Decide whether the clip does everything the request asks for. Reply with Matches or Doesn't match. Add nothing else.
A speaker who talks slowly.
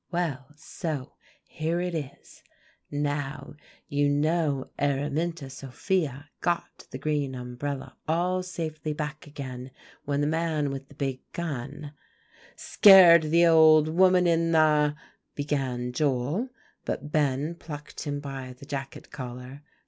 Matches